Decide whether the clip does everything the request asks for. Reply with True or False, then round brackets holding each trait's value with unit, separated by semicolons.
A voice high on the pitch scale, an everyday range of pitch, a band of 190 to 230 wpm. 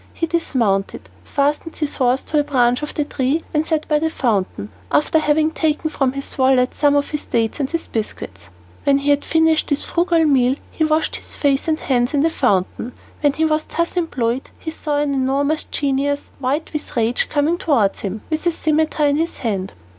True (285 Hz; 3.5 semitones; 200 wpm)